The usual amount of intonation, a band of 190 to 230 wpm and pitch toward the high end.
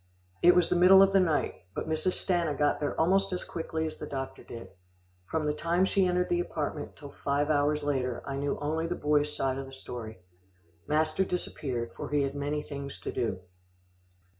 No: average, 3.8 semitones; average, 200 wpm; medium, 150 Hz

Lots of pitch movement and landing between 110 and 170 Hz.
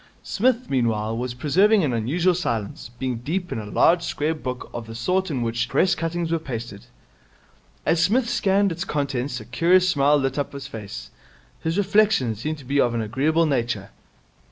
Yes: wide, 6.8 semitones; medium, 140 Hz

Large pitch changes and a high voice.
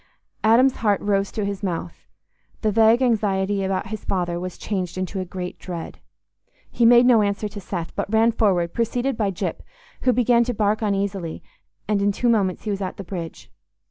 No: average, 3.1 semitones; high, 200 Hz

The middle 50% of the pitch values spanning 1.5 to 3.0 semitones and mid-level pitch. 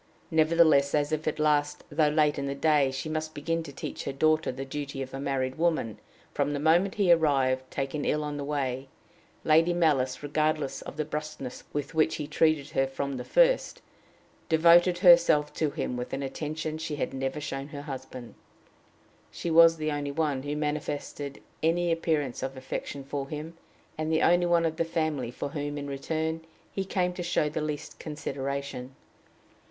Yes: narrow, 2.5 semitones; medium, 150 Hz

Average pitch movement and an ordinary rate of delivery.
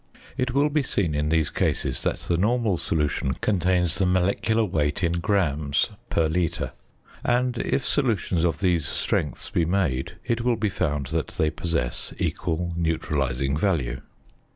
Yes: average, 5.0 semitones; average, 155 wpm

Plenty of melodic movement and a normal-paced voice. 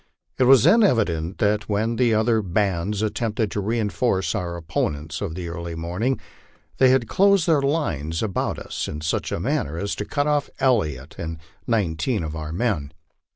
Yes: wide, 6.2 semitones; average, 175 wpm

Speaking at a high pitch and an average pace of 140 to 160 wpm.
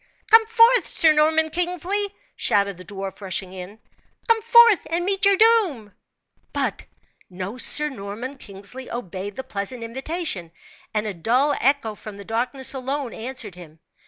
Yes: very high, 255 Hz; average, 150 wpm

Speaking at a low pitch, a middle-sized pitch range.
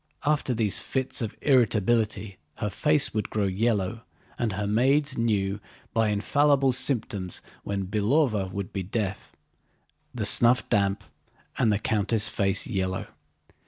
Yes: low, 110 Hz; average, 3.6 semitones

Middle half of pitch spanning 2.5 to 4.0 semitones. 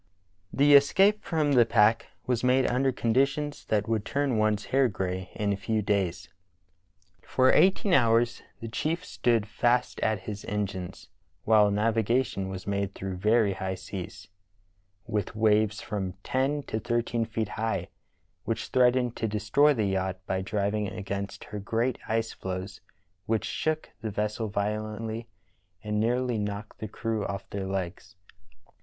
Yes: average, 3.3 semitones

